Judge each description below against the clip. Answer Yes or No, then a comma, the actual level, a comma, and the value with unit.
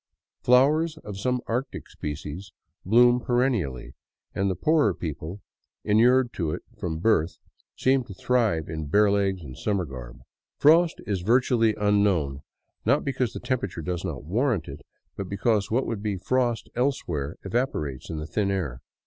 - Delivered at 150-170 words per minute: Yes, average, 165 wpm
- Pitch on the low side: Yes, low, 100 Hz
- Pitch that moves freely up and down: Yes, wide, 7.1 semitones